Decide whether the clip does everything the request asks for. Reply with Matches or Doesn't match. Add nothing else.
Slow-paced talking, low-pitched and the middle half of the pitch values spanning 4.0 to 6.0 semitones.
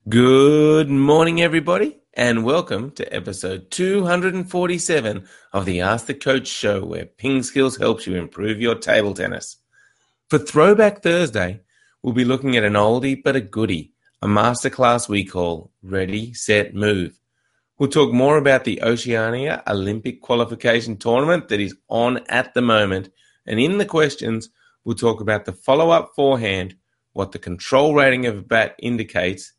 Doesn't match